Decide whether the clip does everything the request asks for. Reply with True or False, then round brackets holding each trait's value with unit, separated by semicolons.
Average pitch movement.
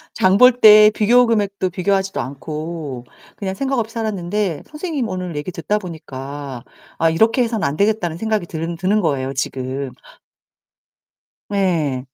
False (6.0 semitones)